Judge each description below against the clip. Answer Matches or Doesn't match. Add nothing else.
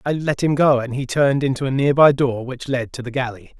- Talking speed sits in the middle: Doesn't match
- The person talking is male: Matches